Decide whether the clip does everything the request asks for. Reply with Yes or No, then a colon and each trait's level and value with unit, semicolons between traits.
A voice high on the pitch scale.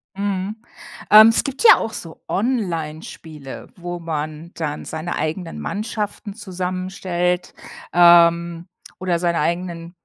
No: medium, 175 Hz